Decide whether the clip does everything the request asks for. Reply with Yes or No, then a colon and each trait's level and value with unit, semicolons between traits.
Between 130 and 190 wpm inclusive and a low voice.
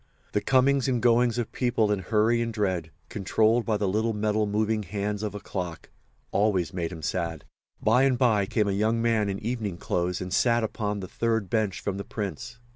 No: average, 200 wpm; low, 105 Hz